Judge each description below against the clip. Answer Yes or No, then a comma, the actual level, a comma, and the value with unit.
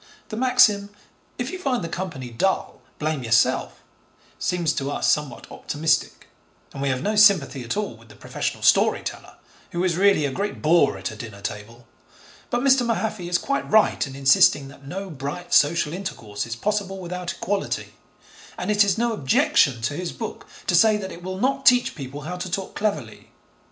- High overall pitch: No, medium, 175 Hz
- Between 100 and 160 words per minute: No, average, 185 wpm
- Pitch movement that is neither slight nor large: No, wide, 7.1 semitones